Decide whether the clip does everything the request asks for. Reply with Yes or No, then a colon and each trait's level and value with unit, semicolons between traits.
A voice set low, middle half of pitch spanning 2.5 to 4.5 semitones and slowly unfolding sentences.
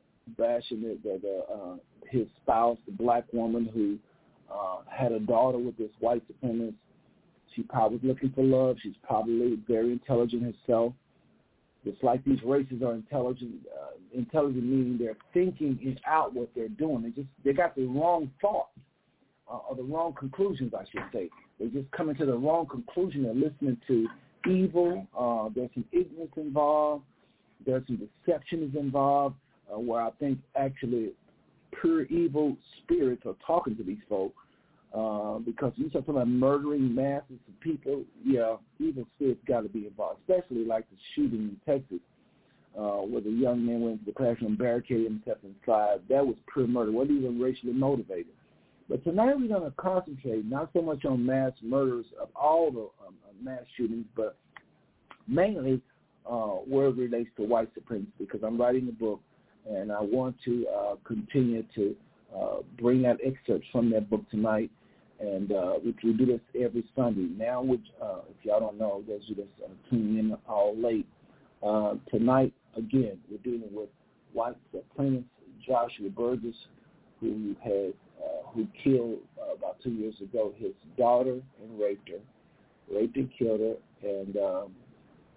No: low, 125 Hz; average, 3.3 semitones; average, 170 wpm